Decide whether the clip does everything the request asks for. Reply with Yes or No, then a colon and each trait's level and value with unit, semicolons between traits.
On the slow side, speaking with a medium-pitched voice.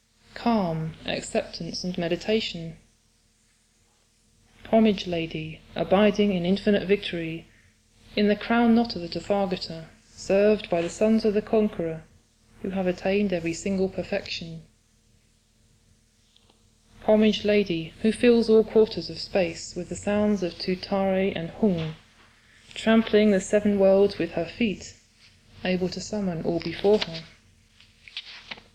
Yes: slow, 120 wpm; medium, 175 Hz